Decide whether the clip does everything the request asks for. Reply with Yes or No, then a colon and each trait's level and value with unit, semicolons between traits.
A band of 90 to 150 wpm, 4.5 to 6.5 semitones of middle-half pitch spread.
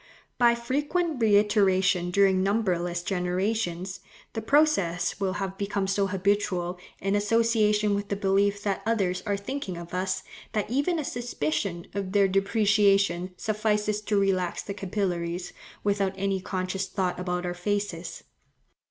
No: slow, 135 wpm; narrow, 2.4 semitones